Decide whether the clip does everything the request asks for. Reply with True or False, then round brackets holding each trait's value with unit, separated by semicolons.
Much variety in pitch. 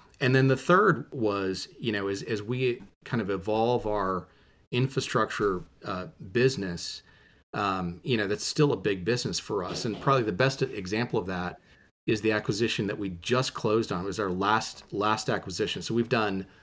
False (4.1 semitones)